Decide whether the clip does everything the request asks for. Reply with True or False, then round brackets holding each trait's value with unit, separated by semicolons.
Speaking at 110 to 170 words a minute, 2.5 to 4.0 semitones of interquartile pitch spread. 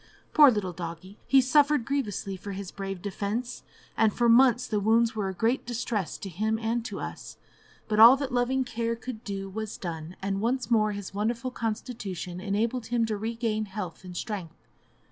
False (185 wpm; 3.5 semitones)